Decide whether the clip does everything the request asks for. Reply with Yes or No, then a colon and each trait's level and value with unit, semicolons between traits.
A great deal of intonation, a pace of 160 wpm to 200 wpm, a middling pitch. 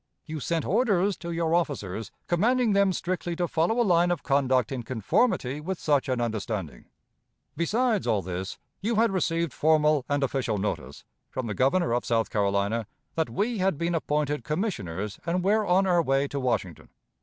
Yes: wide, 7.3 semitones; average, 175 wpm; medium, 155 Hz